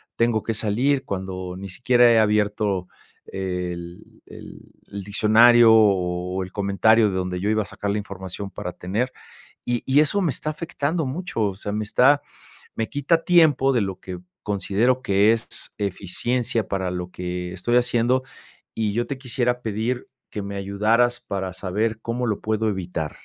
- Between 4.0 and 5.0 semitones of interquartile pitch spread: Yes, average, 4.3 semitones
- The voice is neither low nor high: No, low, 105 Hz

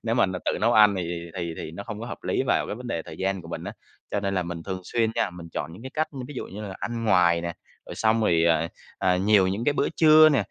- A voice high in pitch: No, very low, 95 Hz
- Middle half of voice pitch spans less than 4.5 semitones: No, average, 5.0 semitones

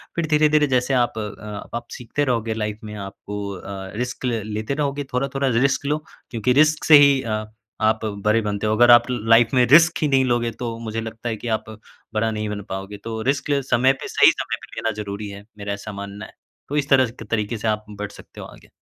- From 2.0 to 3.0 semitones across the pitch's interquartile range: No, average, 3.7 semitones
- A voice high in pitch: No, low, 115 Hz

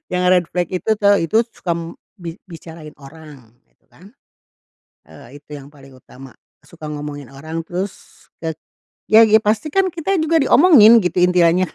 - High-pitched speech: No, medium, 175 Hz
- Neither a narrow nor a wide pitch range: No, wide, 5.8 semitones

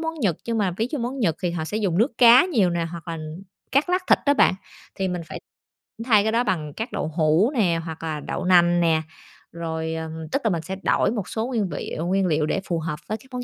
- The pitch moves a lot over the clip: Yes, wide, 5.9 semitones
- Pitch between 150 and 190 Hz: Yes, medium, 185 Hz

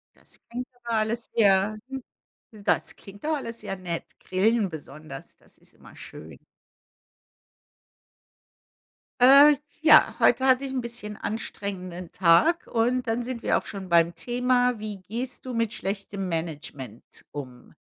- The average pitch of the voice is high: Yes, high, 215 Hz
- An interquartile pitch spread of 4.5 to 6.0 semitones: Yes, average, 5.1 semitones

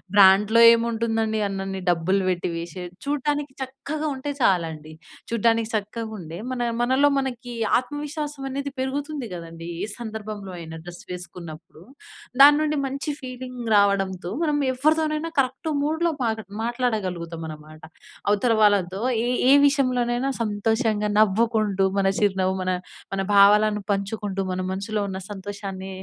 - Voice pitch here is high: Yes, high, 220 Hz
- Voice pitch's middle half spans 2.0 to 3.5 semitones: No, average, 5.3 semitones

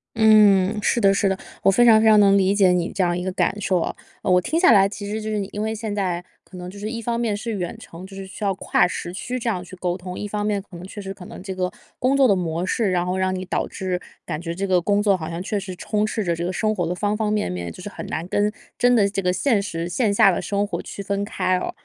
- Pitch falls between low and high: No, high, 195 Hz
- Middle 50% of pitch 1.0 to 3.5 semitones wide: Yes, narrow, 2.6 semitones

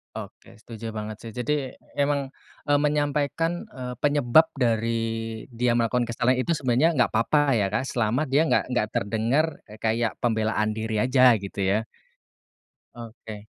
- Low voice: Yes, low, 120 Hz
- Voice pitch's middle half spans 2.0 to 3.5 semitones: No, average, 4.3 semitones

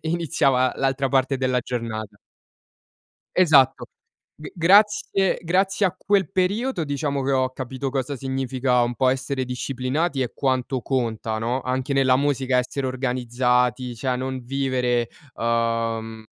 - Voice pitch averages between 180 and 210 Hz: No, low, 130 Hz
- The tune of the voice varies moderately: No, narrow, 2.1 semitones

